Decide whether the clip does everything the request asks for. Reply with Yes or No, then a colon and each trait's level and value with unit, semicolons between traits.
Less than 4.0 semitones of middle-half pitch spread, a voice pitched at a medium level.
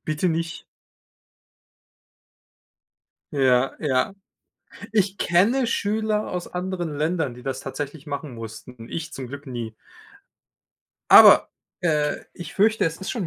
No: wide, 5.6 semitones; medium, 160 Hz